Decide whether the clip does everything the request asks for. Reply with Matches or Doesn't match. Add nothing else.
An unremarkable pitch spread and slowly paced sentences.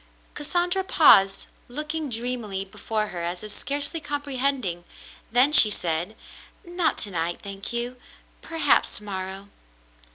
Doesn't match